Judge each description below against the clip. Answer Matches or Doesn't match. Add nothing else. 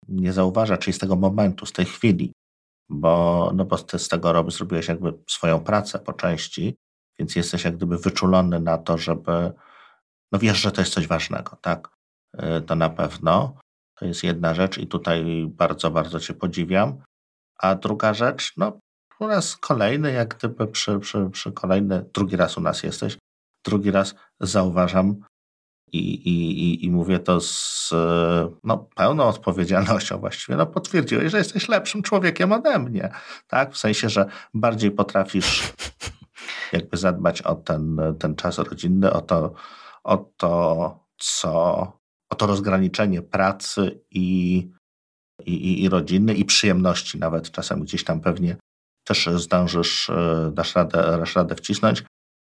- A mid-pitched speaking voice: Doesn't match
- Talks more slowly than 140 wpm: Doesn't match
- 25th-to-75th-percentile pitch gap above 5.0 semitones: Doesn't match